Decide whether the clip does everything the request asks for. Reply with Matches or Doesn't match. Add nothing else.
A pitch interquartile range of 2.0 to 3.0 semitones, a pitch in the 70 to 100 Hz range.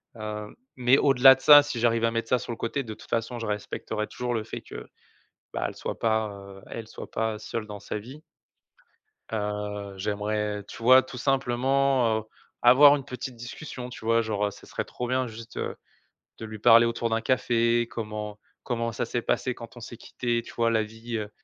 Doesn't match